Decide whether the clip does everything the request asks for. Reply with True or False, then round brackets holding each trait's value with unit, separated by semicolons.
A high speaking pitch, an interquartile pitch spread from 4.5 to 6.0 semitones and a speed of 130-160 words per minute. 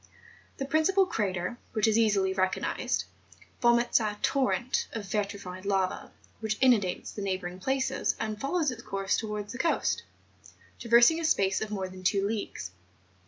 False (215 Hz; 4.0 semitones; 155 wpm)